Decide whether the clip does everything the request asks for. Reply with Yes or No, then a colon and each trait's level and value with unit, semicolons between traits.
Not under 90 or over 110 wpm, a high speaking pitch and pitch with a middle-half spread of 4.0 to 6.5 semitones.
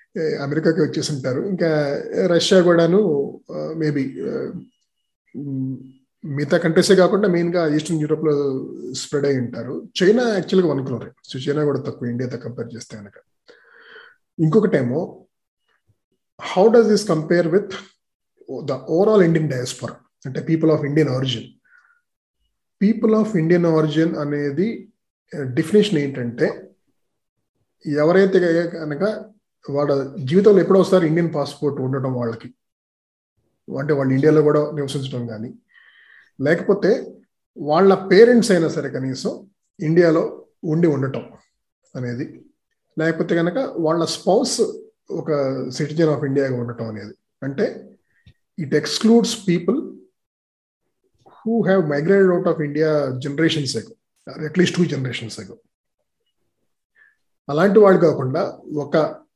No: average, 105 wpm; medium, 155 Hz; wide, 5.4 semitones